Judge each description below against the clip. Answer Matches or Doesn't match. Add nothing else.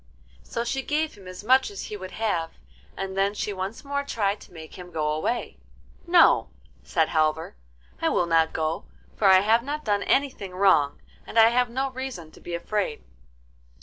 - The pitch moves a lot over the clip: Matches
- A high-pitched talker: Matches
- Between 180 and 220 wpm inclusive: Matches